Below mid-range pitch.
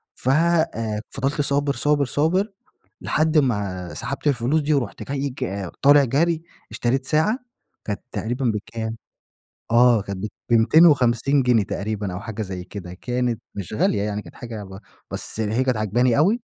Yes: low, 120 Hz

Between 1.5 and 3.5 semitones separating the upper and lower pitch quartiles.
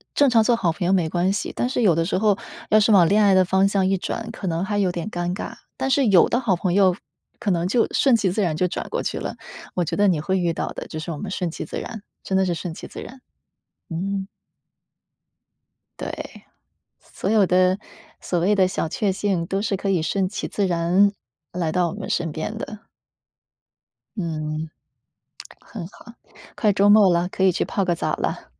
Yes: average, 2.9 semitones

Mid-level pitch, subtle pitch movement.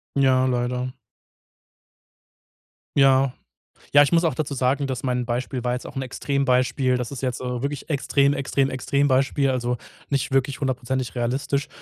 No: low, 130 Hz; narrow, 1.7 semitones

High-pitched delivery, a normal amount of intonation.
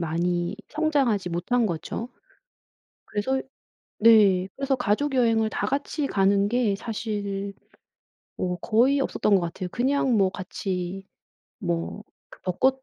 Yes: high, 210 Hz; average, 5.0 semitones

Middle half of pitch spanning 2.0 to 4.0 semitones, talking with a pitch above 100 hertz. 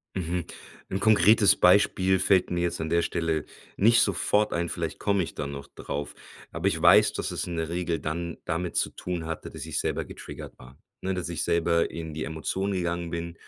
No: narrow, 2.4 semitones; very low, 85 Hz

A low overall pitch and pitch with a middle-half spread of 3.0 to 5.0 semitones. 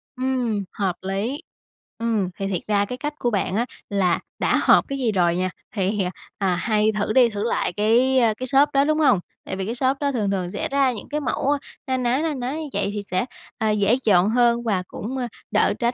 No: high, 225 Hz; average, 4.5 semitones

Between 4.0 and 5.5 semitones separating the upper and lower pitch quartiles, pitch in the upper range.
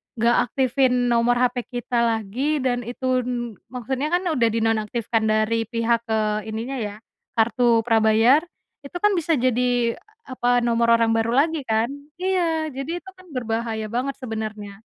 No: narrow, 2.5 semitones; high, 240 Hz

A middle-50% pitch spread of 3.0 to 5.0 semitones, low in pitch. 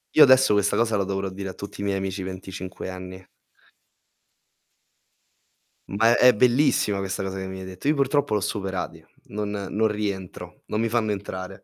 No: narrow, 2.6 semitones; low, 100 Hz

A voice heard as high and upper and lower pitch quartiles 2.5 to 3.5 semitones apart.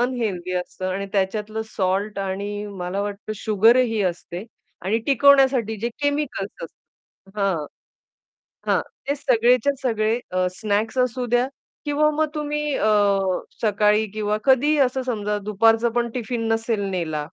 No: high, 220 Hz; average, 4.0 semitones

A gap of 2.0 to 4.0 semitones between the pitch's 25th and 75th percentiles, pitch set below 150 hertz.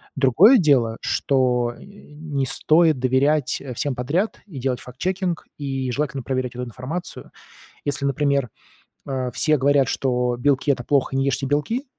Yes: average, 2.8 semitones; low, 135 Hz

